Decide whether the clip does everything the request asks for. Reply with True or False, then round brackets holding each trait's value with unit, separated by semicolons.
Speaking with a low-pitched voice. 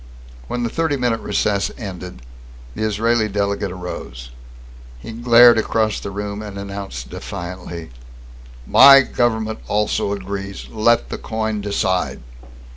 True (105 Hz)